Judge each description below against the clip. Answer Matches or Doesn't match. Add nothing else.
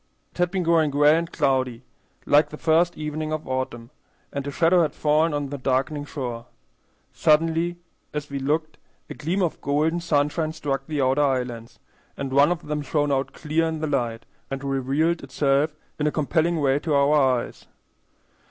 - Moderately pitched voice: Matches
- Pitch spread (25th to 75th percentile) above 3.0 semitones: Doesn't match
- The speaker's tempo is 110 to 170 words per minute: Doesn't match